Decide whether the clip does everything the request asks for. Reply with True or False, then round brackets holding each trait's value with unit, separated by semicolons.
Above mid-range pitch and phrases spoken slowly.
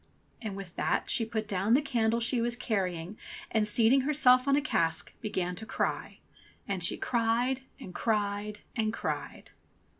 False (220 Hz; 160 wpm)